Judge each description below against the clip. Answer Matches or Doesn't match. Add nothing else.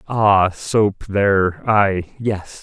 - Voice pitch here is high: Doesn't match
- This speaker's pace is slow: Matches